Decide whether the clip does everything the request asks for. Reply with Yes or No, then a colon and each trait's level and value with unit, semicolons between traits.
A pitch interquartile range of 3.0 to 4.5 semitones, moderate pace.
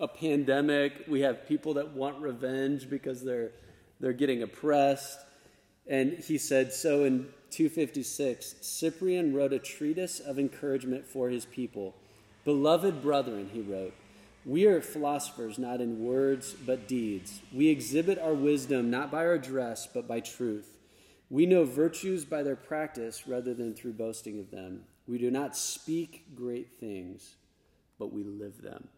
Yes: average, 4.0 semitones; average, 150 wpm